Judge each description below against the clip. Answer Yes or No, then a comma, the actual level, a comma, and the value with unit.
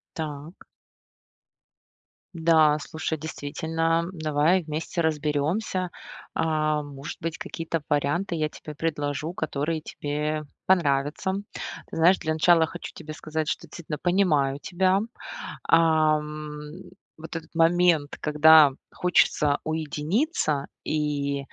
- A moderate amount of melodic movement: No, narrow, 1.8 semitones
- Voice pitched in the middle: Yes, medium, 155 Hz